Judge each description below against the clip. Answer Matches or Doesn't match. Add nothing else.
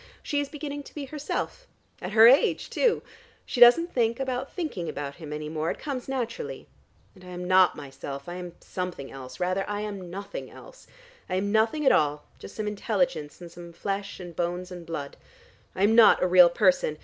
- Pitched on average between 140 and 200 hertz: Matches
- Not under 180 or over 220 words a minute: Matches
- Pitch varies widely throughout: Matches